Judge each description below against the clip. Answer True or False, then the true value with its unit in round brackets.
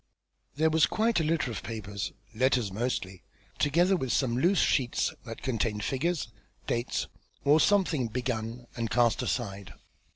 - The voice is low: True (125 Hz)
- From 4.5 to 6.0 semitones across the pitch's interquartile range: True (5.5 semitones)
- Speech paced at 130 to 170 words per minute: True (140 wpm)